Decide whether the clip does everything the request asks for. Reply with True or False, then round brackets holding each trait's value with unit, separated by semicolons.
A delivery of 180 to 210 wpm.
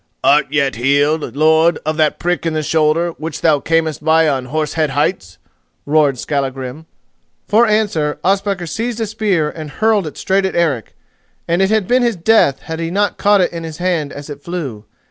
True (195 wpm)